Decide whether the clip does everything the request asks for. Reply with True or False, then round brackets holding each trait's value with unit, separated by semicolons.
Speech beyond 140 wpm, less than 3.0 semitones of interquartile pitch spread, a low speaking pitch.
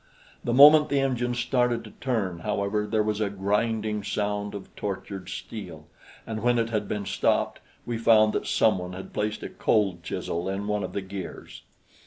True (185 wpm; 2.6 semitones; 105 Hz)